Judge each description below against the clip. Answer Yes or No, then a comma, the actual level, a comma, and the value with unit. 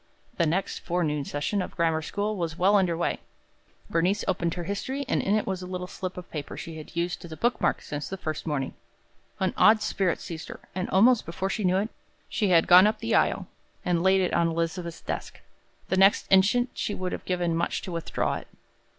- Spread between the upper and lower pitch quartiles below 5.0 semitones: Yes, average, 2.8 semitones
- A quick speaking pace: Yes, fast, 225 wpm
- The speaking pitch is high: No, medium, 180 Hz